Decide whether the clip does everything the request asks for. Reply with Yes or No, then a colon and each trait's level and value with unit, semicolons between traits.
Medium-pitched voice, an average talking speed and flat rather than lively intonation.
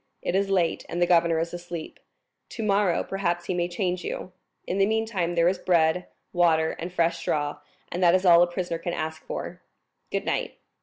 Yes: medium, 175 Hz; average, 190 wpm; narrow, 1.6 semitones